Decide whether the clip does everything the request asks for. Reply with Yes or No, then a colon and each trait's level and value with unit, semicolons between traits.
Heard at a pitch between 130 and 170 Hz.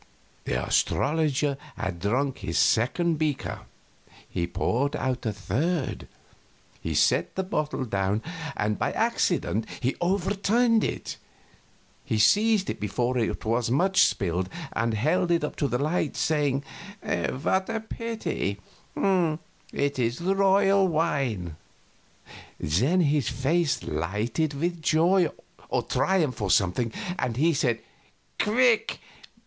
Yes: medium, 140 Hz